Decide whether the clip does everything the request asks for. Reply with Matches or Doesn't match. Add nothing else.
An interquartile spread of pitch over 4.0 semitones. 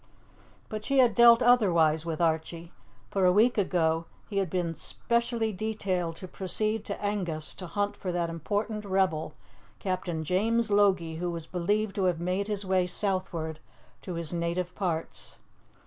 Doesn't match